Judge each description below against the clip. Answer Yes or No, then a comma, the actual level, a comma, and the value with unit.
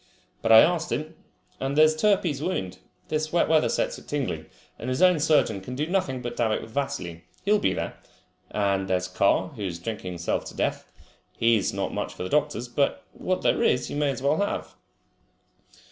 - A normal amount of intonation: No, wide, 6.9 semitones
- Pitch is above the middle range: No, low, 135 Hz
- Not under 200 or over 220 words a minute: Yes, fast, 205 wpm